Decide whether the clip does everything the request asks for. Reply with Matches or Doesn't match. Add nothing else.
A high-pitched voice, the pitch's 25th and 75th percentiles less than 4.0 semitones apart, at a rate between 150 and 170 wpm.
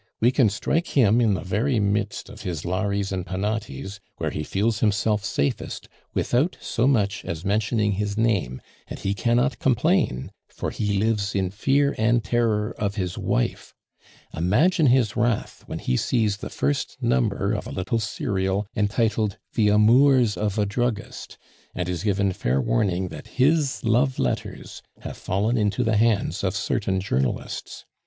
Doesn't match